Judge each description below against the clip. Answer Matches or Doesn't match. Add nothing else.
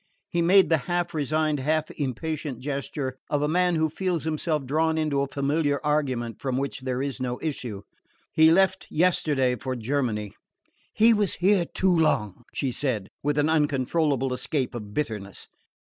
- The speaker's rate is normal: Matches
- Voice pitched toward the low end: Doesn't match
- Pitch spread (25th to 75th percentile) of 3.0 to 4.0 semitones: Matches